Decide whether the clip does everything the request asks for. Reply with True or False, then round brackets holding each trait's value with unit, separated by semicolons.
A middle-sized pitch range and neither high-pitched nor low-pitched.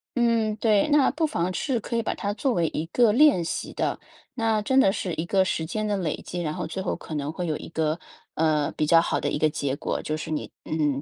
False (6.2 semitones; 180 Hz)